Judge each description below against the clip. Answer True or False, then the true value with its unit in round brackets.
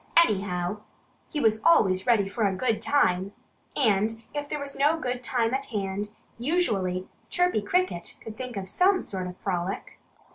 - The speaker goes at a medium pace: True (160 wpm)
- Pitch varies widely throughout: True (6.3 semitones)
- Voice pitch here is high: True (220 Hz)